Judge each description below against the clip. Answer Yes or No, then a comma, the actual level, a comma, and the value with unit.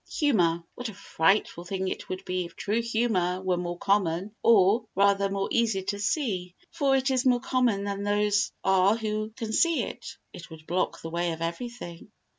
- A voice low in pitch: No, high, 200 Hz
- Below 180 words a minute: No, average, 190 wpm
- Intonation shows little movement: No, average, 4.2 semitones